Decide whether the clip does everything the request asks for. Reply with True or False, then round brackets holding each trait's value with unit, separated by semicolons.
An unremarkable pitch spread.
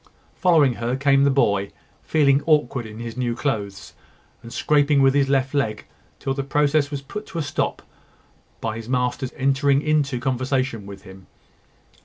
True (3.3 semitones)